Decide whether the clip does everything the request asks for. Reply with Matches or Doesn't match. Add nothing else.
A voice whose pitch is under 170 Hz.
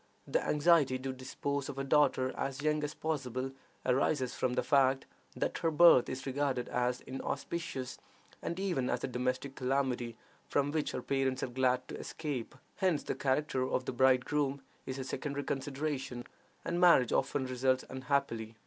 Matches